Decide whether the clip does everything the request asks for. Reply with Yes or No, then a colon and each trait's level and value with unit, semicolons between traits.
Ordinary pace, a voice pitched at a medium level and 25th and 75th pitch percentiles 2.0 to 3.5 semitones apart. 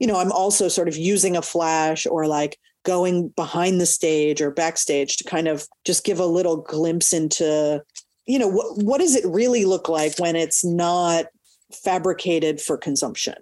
Yes: average, 185 wpm; medium, 170 Hz; narrow, 2.6 semitones